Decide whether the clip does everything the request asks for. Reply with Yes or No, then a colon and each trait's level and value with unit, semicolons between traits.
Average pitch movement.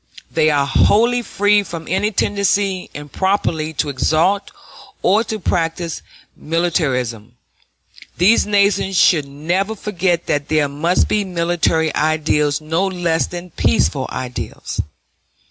Yes: average, 4.5 semitones